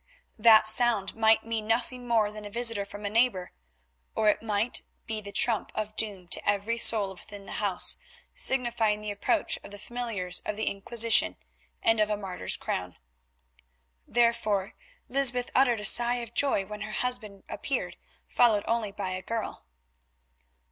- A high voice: Yes, high, 215 Hz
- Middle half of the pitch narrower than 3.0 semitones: Yes, narrow, 2.5 semitones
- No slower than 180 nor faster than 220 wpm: No, average, 160 wpm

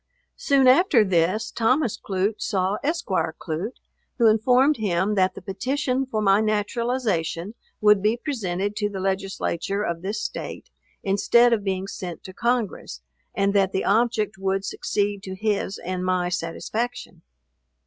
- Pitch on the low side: No, high, 205 Hz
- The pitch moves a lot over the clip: No, average, 3.6 semitones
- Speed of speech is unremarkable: Yes, average, 145 wpm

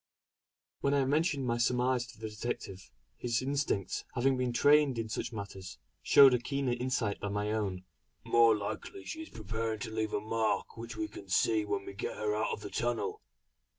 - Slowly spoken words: No, average, 190 wpm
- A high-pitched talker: No, low, 120 Hz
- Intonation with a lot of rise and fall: No, average, 4.6 semitones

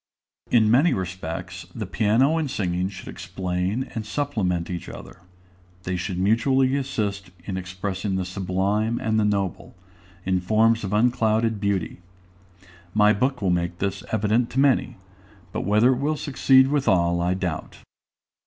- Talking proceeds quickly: No, average, 150 wpm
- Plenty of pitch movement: No, average, 4.2 semitones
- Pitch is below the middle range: Yes, low, 105 Hz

